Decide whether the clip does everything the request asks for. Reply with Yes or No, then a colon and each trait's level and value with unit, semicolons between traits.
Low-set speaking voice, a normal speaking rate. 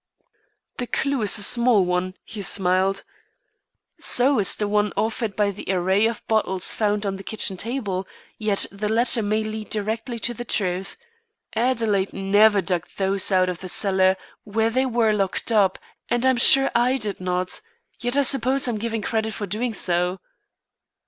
No: high, 210 Hz; average, 170 wpm